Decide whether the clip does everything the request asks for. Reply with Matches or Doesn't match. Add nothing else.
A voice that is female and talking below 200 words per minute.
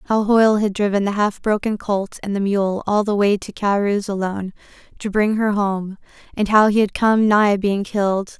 Doesn't match